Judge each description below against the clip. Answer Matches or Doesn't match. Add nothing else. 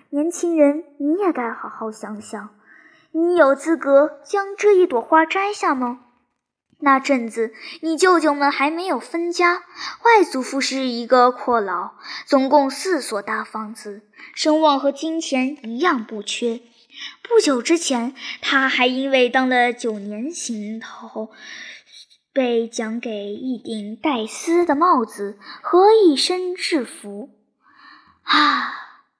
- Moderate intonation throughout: Doesn't match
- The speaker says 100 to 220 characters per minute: Matches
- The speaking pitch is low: Doesn't match